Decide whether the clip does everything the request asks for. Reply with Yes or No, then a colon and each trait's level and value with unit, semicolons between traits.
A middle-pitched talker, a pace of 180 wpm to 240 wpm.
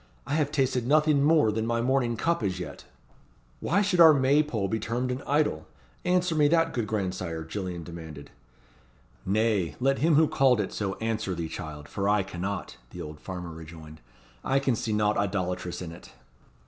No: low, 110 Hz; average, 185 wpm